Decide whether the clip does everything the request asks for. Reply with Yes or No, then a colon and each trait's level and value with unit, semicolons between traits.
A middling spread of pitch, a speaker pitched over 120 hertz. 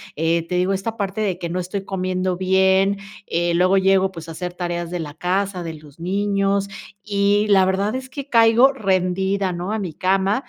No: narrow, 2.0 semitones; high, 190 Hz